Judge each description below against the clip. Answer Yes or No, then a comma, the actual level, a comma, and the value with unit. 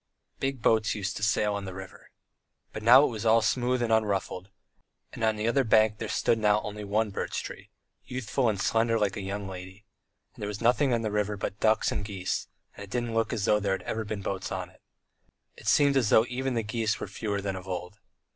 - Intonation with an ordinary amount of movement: No, narrow, 2.3 semitones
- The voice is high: No, low, 105 Hz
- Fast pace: Yes, fast, 230 wpm